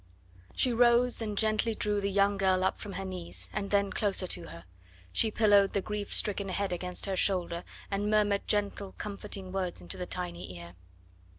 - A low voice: No, high, 200 Hz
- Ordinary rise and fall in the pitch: No, narrow, 2.2 semitones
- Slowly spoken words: No, average, 185 wpm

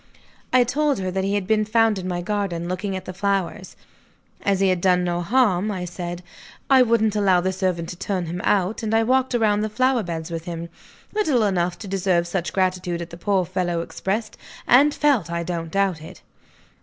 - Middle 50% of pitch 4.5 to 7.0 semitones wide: No, average, 3.4 semitones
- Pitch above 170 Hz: Yes, high, 190 Hz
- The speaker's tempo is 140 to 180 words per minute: No, fast, 205 wpm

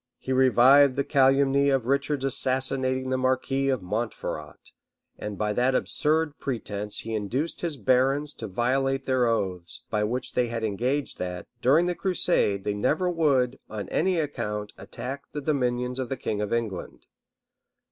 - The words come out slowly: No, average, 155 wpm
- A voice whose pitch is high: No, low, 130 Hz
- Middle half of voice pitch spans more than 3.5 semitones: Yes, average, 4.0 semitones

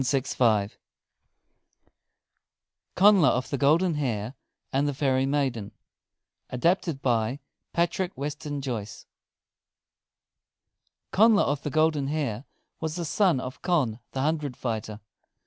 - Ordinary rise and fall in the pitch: Yes, average, 4.1 semitones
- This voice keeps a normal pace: No, slow, 105 wpm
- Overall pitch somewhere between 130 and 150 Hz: Yes, medium, 140 Hz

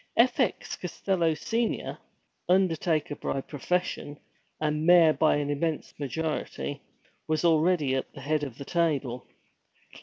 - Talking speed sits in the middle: No, slow, 125 wpm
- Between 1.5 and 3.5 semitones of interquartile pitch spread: Yes, average, 3.2 semitones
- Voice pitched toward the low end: No, medium, 155 Hz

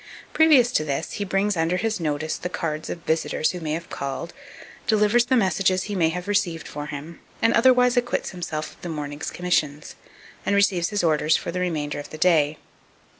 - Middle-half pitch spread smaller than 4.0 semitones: No, average, 4.8 semitones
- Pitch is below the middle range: No, medium, 175 Hz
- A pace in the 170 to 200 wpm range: Yes, average, 195 wpm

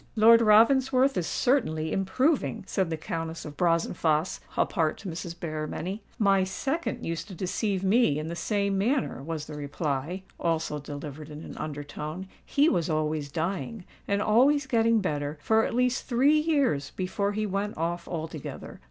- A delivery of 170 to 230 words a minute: No, average, 160 wpm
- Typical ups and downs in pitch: No, wide, 6.1 semitones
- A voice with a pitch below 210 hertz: Yes, medium, 185 Hz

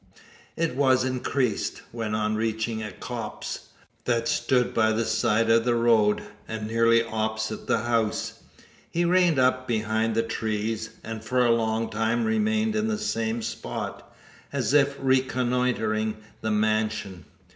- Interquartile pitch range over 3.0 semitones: No, narrow, 2.6 semitones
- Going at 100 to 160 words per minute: Yes, average, 145 wpm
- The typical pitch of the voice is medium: No, low, 115 Hz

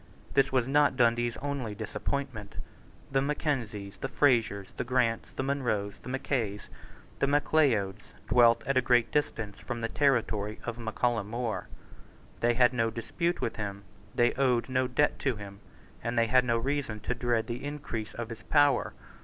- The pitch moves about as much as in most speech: Yes, average, 3.2 semitones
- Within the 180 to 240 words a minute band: No, average, 170 wpm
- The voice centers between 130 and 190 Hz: No, low, 120 Hz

